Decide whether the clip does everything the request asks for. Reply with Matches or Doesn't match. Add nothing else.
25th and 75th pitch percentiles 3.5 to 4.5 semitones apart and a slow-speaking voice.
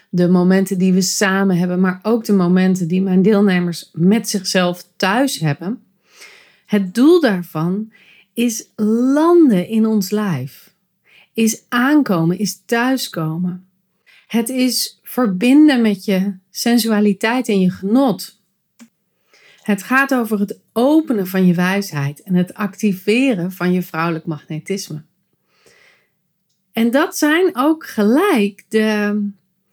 Matches